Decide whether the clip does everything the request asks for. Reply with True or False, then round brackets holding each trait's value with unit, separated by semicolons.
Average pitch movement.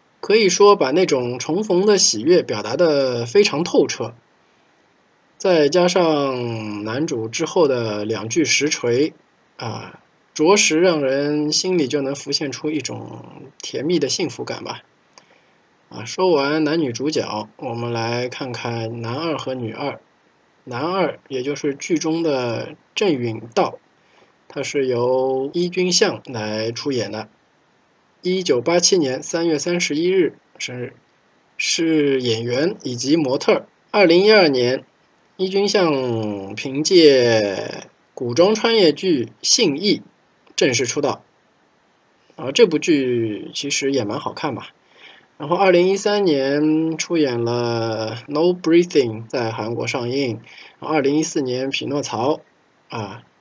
False (6.0 semitones)